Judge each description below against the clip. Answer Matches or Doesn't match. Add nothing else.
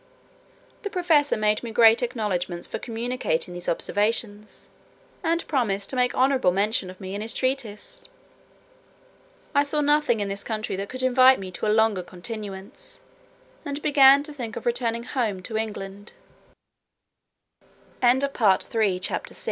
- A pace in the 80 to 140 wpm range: Matches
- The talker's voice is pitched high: Matches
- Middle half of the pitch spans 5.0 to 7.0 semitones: Doesn't match